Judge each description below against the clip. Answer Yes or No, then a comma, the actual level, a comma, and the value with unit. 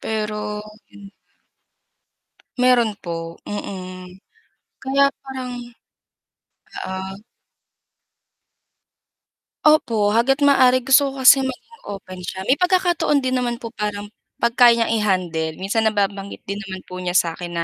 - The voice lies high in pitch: Yes, high, 215 Hz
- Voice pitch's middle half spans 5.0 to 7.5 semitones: Yes, wide, 5.5 semitones